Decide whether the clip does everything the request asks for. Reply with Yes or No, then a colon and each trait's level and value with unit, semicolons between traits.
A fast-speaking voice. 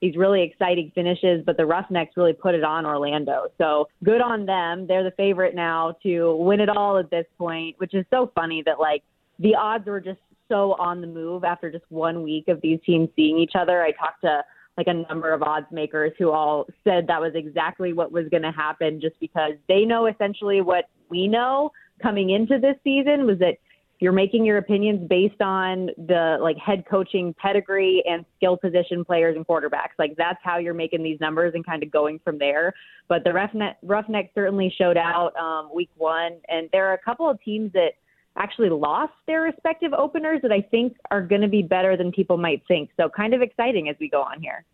Yes: fast, 215 wpm